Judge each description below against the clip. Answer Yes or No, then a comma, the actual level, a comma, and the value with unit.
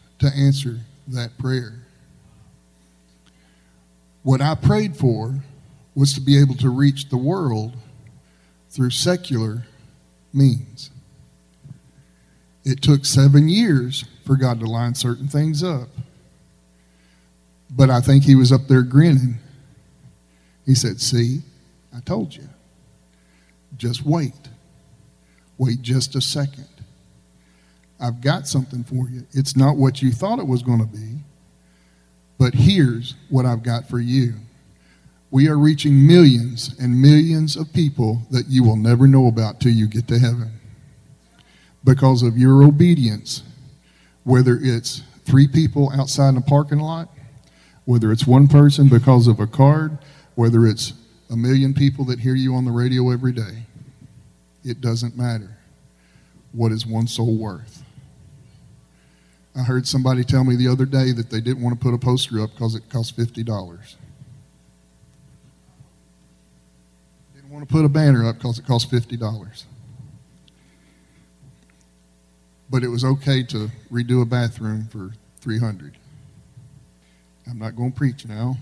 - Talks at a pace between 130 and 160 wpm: Yes, average, 140 wpm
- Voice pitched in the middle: No, low, 125 Hz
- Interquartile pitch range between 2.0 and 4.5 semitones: Yes, average, 3.7 semitones